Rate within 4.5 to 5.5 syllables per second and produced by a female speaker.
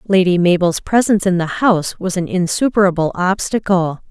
Yes: 5.4 syllables/s; female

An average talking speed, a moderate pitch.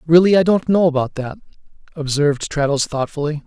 Yes: average, 155 wpm; medium, 155 Hz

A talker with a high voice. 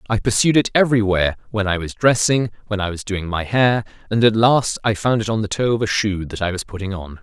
No: low, 105 Hz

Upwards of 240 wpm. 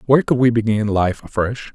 No: fast, 205 wpm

